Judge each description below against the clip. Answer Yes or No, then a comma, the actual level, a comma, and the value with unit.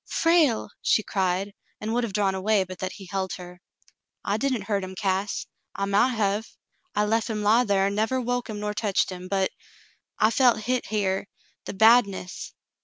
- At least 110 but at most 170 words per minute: No, average, 200 wpm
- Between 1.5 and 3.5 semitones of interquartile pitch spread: Yes, narrow, 2.6 semitones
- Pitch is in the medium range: No, high, 205 Hz